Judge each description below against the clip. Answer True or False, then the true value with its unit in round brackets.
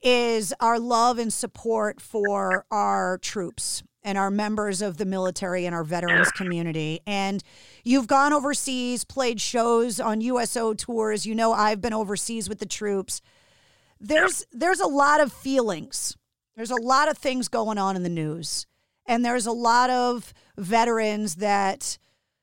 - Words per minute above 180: False (155 wpm)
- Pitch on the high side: True (220 Hz)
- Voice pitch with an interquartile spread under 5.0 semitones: True (3.8 semitones)